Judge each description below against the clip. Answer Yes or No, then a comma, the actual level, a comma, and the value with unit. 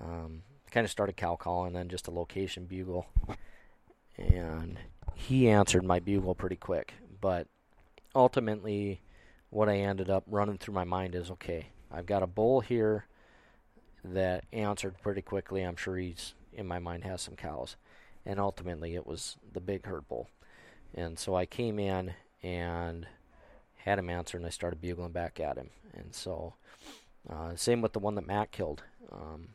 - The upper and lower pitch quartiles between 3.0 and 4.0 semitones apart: No, narrow, 2.6 semitones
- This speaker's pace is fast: No, average, 170 wpm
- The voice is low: Yes, very low, 95 Hz